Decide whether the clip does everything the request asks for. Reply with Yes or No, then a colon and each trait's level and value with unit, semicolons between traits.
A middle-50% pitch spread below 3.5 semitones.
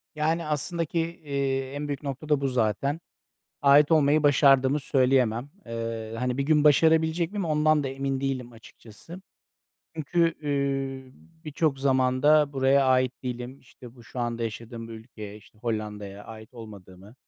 No: average, 4.0 semitones